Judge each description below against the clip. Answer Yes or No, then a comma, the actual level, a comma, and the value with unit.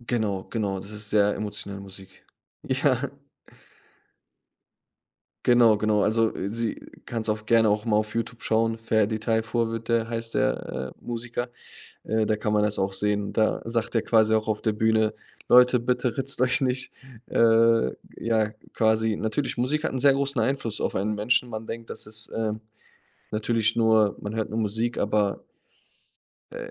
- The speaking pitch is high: No, low, 110 Hz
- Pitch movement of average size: No, narrow, 1.6 semitones